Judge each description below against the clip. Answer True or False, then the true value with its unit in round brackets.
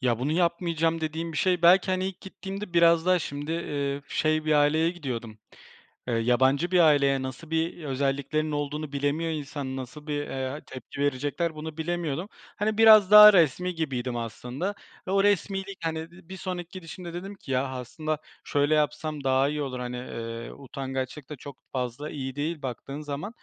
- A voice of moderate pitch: True (150 Hz)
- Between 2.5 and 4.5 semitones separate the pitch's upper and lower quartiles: True (4.0 semitones)